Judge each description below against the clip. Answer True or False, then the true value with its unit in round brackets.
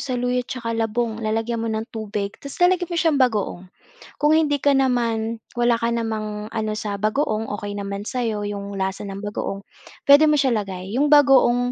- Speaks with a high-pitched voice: True (225 Hz)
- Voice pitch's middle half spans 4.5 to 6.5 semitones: False (3.4 semitones)